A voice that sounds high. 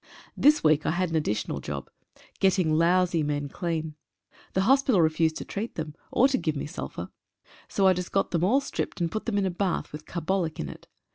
No: medium, 170 Hz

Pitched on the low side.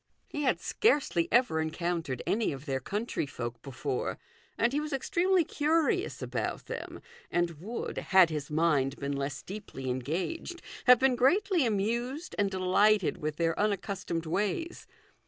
No: high, 195 Hz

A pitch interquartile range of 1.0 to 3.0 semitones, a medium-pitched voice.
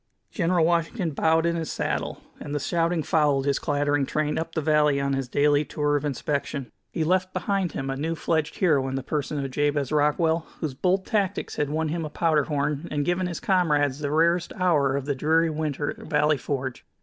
Yes: narrow, 2.6 semitones; medium, 150 Hz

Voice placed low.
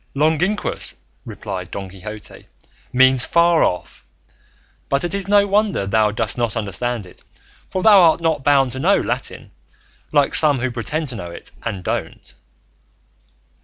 Yes: low, 130 Hz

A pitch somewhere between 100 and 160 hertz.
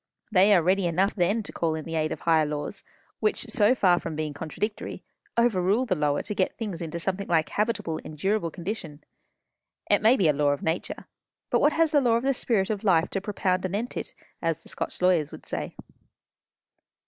No: medium, 185 Hz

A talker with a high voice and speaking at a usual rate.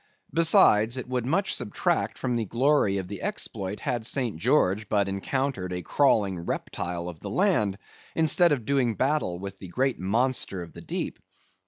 No: low, 115 Hz; average, 170 wpm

